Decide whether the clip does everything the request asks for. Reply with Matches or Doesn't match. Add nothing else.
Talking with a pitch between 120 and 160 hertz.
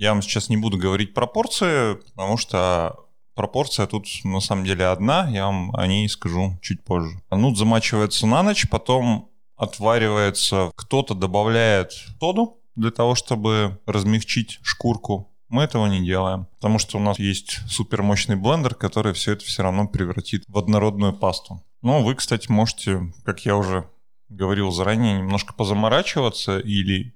Doesn't match